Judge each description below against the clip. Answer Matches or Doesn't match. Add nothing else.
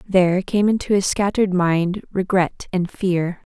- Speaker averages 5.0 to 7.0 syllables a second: Doesn't match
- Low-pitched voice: Doesn't match